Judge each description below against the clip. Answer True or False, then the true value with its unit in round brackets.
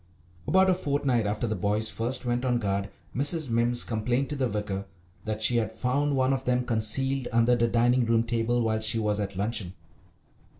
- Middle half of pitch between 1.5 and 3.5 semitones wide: True (2.8 semitones)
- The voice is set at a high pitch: False (120 Hz)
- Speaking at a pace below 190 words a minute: False (195 wpm)